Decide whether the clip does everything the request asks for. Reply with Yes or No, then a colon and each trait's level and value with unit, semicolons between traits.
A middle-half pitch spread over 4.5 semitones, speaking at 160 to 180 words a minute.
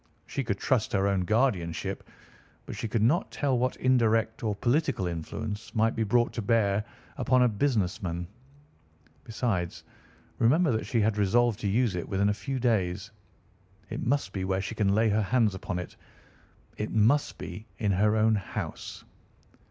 No: average, 3.5 semitones; average, 170 wpm